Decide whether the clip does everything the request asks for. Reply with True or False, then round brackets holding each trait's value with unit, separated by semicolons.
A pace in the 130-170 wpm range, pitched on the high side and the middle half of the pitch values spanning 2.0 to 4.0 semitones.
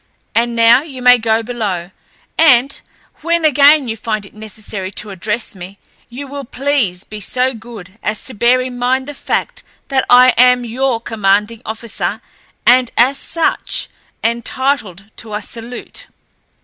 True (150 wpm; 235 Hz; 3.4 semitones)